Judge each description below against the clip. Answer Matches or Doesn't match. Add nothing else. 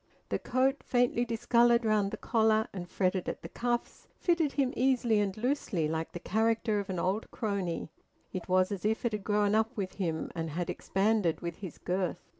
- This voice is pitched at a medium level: Doesn't match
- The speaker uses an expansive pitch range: Doesn't match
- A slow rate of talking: Doesn't match